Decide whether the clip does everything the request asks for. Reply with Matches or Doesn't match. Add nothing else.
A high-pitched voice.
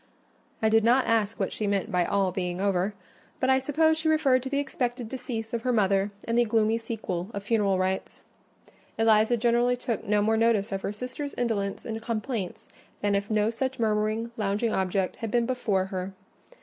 Matches